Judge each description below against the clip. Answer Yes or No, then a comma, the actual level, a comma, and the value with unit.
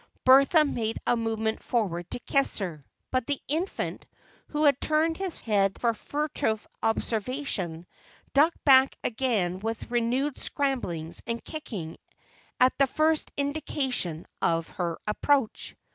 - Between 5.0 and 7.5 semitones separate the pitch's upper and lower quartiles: Yes, wide, 5.5 semitones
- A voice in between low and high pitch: No, high, 245 Hz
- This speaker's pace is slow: Yes, slow, 130 wpm